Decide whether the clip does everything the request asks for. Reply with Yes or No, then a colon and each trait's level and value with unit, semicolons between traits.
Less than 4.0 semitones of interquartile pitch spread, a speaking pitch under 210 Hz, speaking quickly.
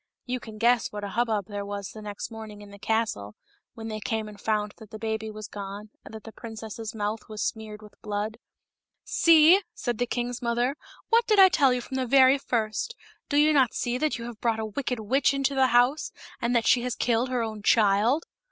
No: average, 2.9 semitones; high, 225 Hz; fast, 230 wpm